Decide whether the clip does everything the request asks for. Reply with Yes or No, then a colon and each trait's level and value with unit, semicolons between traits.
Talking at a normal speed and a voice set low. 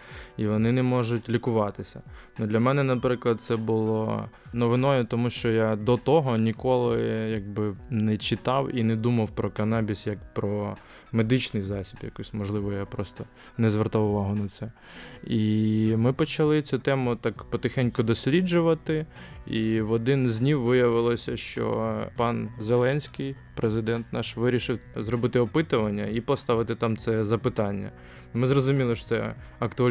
Yes: average, 140 wpm; low, 115 Hz